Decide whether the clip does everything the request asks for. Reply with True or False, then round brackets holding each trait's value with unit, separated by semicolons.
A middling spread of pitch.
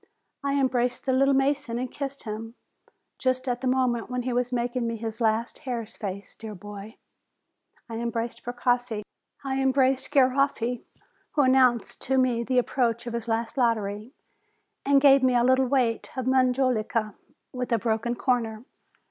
False (2.2 semitones)